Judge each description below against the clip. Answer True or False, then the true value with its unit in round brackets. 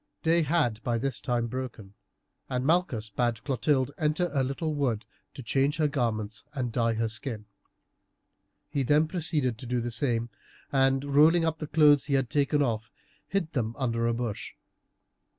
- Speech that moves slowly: False (170 wpm)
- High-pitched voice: False (130 Hz)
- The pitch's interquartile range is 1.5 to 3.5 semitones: False (4.2 semitones)